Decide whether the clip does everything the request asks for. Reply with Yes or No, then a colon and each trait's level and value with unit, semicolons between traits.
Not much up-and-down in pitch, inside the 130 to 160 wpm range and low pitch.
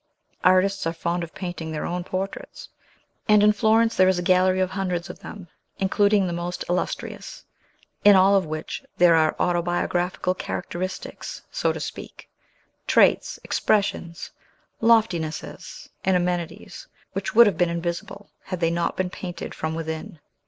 No: narrow, 2.2 semitones; average, 150 wpm; medium, 180 Hz